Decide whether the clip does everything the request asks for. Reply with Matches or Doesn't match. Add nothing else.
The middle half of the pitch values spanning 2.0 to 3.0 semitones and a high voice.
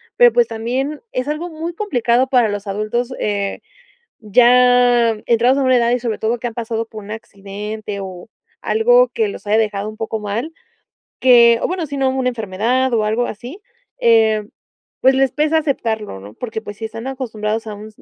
Doesn't match